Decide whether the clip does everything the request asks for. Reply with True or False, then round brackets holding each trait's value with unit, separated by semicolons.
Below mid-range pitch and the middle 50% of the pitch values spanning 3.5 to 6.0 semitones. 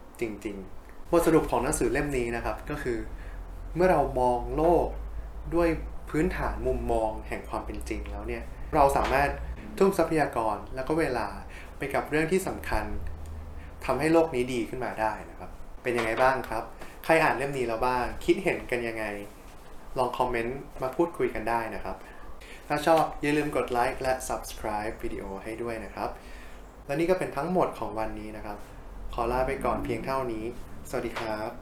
True (115 Hz; 5.5 semitones)